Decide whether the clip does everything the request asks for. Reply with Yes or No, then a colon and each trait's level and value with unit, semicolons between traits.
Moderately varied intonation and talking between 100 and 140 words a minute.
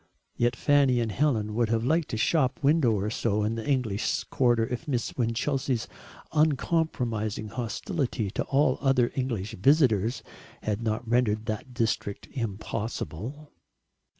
Yes: average, 3.8 semitones; slow, 135 wpm